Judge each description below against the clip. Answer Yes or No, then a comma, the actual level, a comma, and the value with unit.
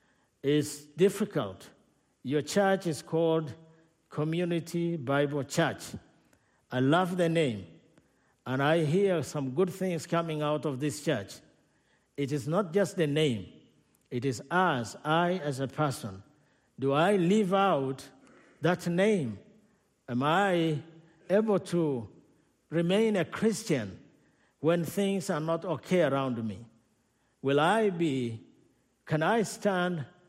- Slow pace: Yes, slow, 125 wpm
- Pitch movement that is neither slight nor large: Yes, average, 4.7 semitones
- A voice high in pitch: No, medium, 160 Hz